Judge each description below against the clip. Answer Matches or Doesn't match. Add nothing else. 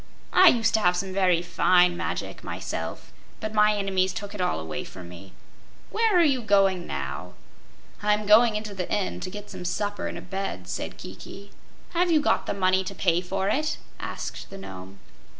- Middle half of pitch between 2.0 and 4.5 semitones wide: Matches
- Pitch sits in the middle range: Doesn't match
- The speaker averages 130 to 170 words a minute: Doesn't match